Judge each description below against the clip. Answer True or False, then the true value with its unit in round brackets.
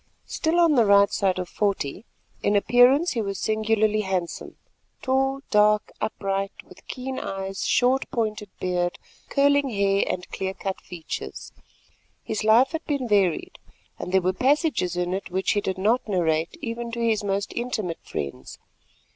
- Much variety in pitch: False (4.4 semitones)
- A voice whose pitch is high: True (210 Hz)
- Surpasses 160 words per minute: False (155 wpm)